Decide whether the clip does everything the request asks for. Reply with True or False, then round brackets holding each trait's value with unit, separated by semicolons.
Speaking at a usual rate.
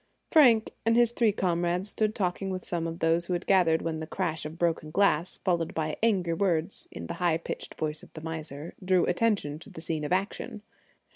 False (210 wpm)